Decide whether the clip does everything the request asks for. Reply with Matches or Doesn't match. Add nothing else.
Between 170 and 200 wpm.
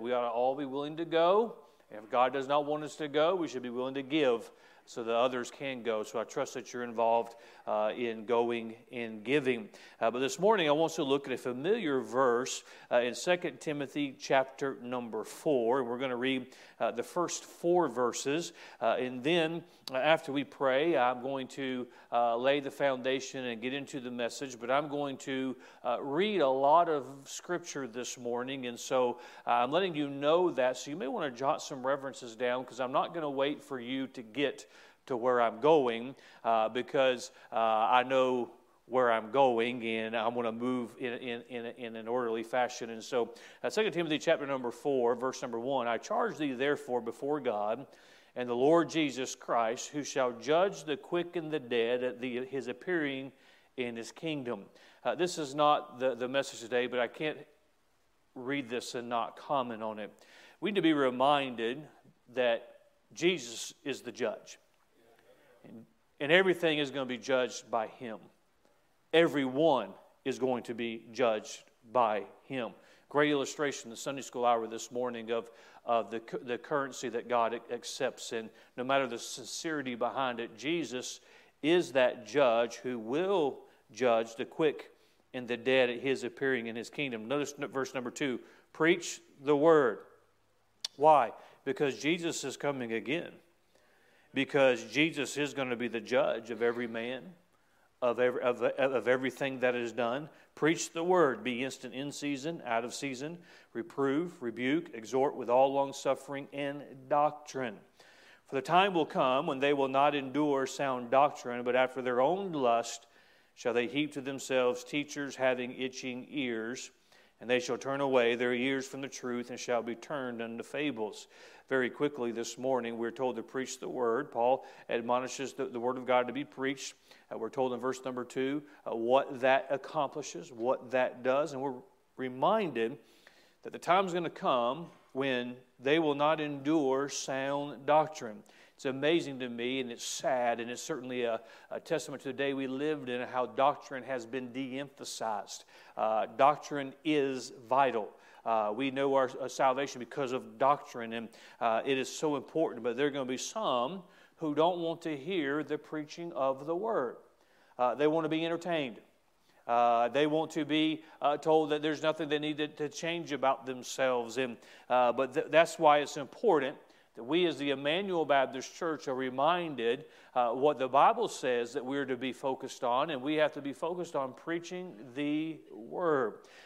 Matches